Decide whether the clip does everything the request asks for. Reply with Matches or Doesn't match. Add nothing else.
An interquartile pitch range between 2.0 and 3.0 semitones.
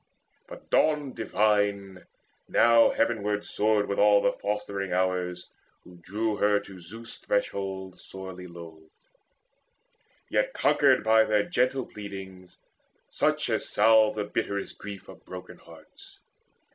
Matches